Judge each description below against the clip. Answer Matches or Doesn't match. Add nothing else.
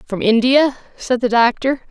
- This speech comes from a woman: Matches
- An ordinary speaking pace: Matches